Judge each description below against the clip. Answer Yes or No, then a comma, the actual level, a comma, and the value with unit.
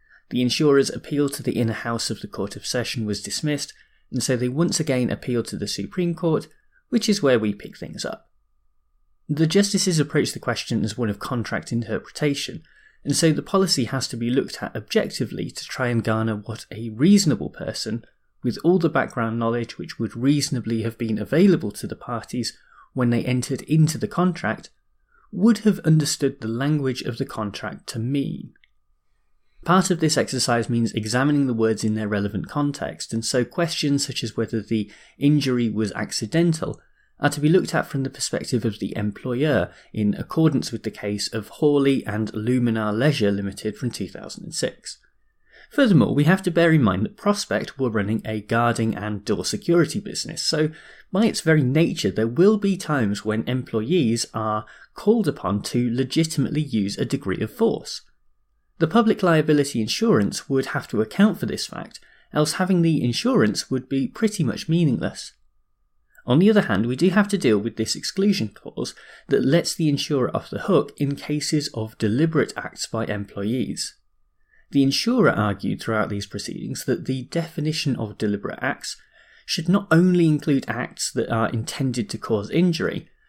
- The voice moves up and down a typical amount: No, wide, 6.3 semitones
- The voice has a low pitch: Yes, low, 130 Hz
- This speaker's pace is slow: No, average, 175 wpm